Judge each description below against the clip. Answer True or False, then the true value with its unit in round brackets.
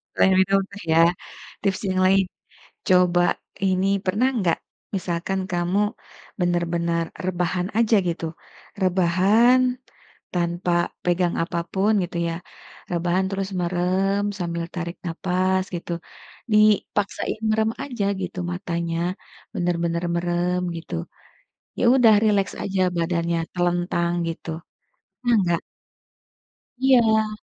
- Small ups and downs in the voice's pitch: True (2.3 semitones)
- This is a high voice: False (180 Hz)